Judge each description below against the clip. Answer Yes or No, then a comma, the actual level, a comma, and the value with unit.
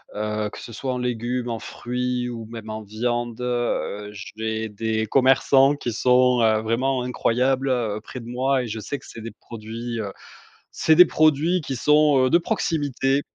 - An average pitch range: Yes, average, 3.1 semitones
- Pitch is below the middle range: Yes, low, 120 Hz